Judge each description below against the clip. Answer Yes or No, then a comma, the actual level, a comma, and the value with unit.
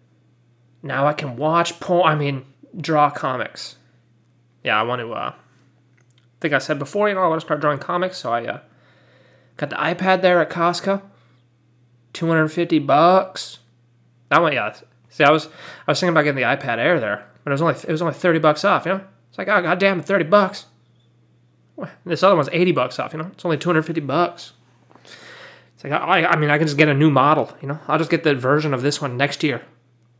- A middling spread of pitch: No, wide, 5.8 semitones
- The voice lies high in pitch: No, medium, 150 Hz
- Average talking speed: No, fast, 220 wpm